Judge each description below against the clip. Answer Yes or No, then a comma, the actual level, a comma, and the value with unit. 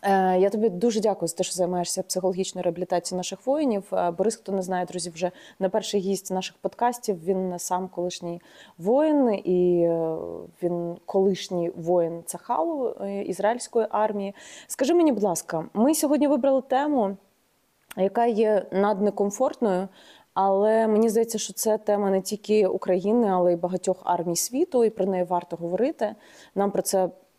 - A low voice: No, high, 195 Hz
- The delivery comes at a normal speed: Yes, average, 145 wpm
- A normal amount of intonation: Yes, average, 3.3 semitones